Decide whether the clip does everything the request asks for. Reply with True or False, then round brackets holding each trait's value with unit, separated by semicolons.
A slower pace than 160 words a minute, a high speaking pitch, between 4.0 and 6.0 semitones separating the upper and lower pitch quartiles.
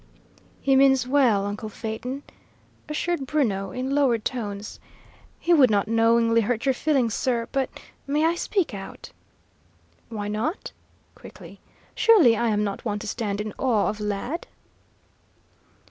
True (140 wpm; 235 Hz; 4.6 semitones)